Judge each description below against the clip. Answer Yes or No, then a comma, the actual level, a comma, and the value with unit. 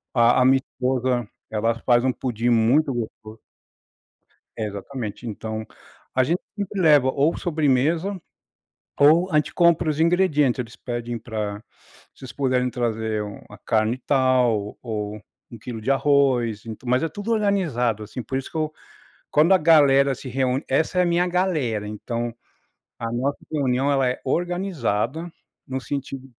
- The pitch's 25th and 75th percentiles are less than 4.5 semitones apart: No, average, 4.8 semitones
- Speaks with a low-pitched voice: Yes, low, 130 Hz